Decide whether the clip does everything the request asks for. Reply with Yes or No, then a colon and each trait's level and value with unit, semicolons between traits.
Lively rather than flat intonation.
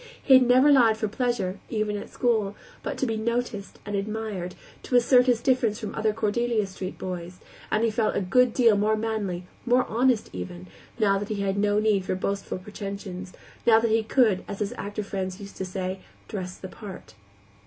No: average, 2.9 semitones